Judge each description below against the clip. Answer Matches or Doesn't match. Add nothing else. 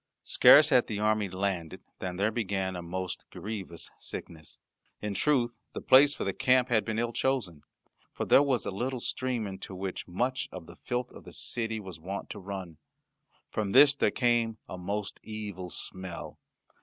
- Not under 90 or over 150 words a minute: Doesn't match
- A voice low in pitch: Matches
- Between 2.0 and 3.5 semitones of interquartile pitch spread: Doesn't match